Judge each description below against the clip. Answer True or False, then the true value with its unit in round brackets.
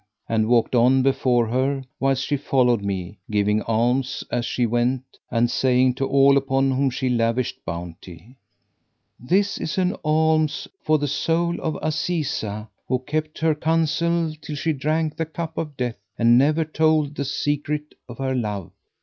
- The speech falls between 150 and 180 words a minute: True (160 wpm)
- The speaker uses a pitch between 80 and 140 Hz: True (135 Hz)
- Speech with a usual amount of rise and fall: True (4.4 semitones)